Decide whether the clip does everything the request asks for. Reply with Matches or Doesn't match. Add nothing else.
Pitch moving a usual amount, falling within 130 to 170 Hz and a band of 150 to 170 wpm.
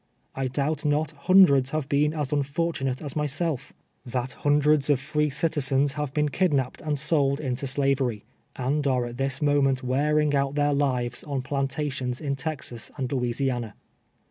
Doesn't match